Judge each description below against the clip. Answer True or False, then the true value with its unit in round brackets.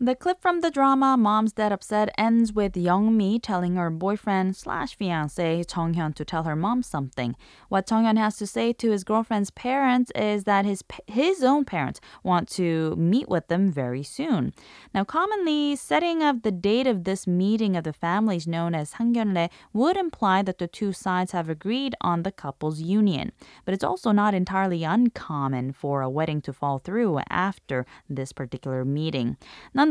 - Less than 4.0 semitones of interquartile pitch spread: False (5.4 semitones)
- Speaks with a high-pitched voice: True (195 Hz)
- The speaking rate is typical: True (180 wpm)